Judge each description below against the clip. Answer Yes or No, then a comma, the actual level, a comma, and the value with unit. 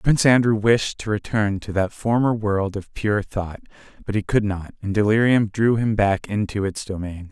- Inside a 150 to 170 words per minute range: No, average, 195 wpm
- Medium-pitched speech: No, low, 105 Hz